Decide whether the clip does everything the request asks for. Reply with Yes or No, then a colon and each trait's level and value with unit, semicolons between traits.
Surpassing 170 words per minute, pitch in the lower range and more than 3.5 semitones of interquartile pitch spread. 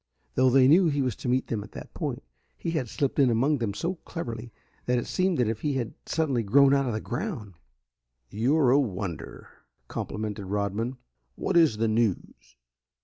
Yes: average, 190 wpm; low, 125 Hz; average, 4.7 semitones